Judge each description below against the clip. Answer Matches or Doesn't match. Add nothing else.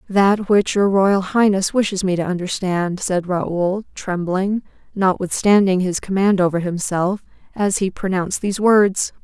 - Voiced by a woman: Matches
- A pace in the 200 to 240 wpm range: Doesn't match